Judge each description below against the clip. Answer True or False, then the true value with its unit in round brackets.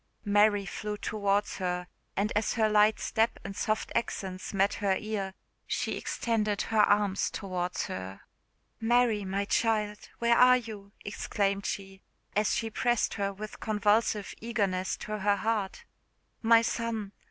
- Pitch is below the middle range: False (210 Hz)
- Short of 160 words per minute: True (140 wpm)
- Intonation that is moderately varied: False (2.0 semitones)